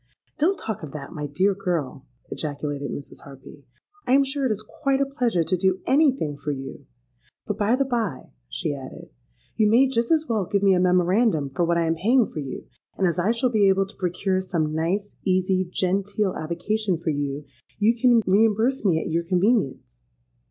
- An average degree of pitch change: No, wide, 5.9 semitones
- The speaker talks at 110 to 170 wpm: No, average, 195 wpm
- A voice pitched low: No, high, 190 Hz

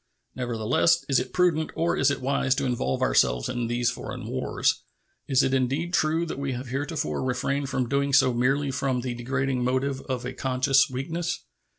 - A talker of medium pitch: No, low, 130 Hz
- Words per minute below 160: No, average, 185 wpm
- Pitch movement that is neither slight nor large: No, narrow, 2.0 semitones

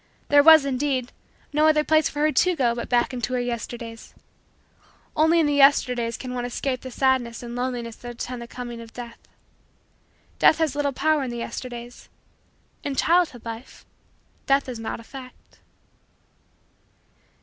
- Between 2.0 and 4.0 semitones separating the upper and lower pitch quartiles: Yes, average, 3.2 semitones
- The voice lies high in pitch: Yes, very high, 255 Hz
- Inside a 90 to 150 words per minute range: No, average, 160 wpm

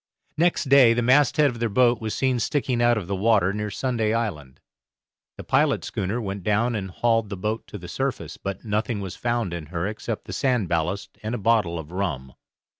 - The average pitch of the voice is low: Yes, low, 110 Hz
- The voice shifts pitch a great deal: No, average, 3.8 semitones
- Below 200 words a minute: No, fast, 205 wpm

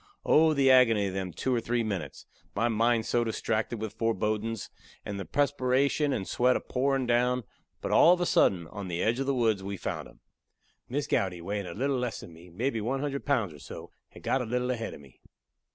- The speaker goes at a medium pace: No, fast, 220 wpm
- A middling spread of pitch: Yes, average, 4.4 semitones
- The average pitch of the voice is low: Yes, low, 115 Hz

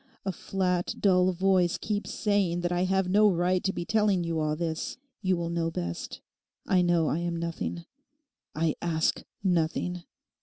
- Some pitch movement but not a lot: No, narrow, 2.0 semitones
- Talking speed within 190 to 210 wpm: No, average, 165 wpm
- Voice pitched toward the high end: No, medium, 175 Hz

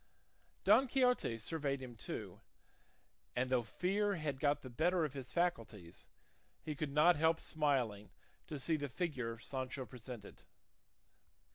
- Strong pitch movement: No, average, 4.7 semitones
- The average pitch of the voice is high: No, medium, 140 Hz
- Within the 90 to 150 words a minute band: Yes, slow, 135 wpm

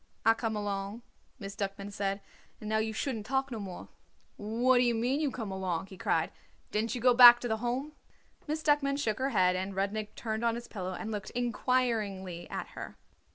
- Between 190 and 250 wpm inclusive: Yes, average, 200 wpm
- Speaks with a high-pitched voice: Yes, high, 220 Hz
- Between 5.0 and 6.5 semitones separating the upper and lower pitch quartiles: No, average, 3.7 semitones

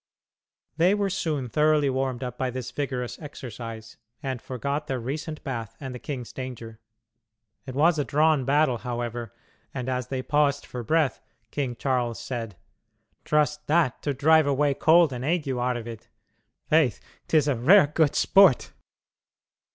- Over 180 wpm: No, average, 145 wpm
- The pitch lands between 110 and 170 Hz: Yes, low, 135 Hz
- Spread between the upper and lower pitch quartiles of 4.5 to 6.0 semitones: No, average, 3.6 semitones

